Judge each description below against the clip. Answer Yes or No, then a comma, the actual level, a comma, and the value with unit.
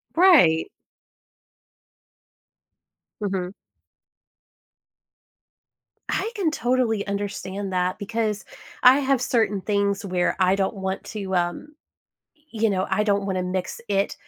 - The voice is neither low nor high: No, high, 200 Hz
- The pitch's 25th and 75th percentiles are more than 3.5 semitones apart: No, average, 3.0 semitones